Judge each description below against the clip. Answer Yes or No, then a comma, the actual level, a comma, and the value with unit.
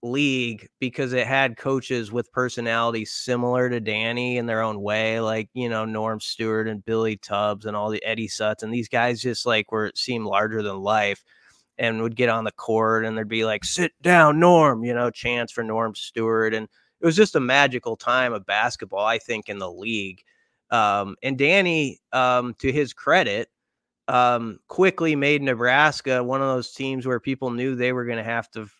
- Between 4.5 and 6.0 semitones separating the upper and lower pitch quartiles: No, average, 2.8 semitones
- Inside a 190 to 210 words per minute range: Yes, average, 195 wpm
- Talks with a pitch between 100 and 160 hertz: Yes, low, 120 Hz